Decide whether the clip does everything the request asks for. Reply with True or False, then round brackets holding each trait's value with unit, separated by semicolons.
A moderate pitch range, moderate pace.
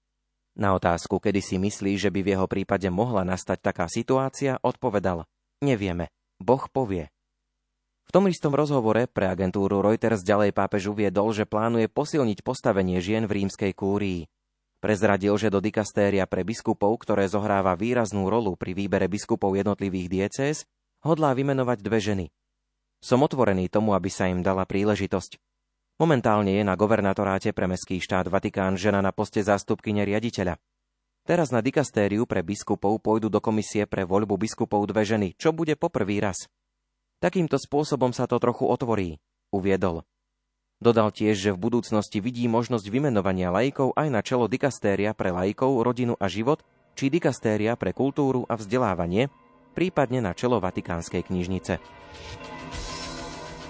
True (3.6 semitones; 145 wpm)